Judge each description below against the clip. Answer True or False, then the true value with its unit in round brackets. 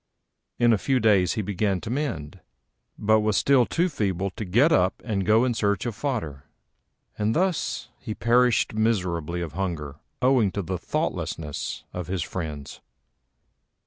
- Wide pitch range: False (5.0 semitones)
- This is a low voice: True (105 Hz)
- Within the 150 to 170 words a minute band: True (155 wpm)